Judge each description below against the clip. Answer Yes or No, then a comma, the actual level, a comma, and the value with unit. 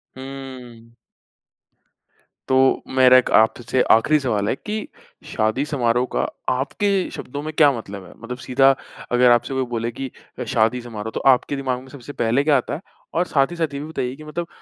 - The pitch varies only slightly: No, average, 3.1 semitones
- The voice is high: No, low, 130 Hz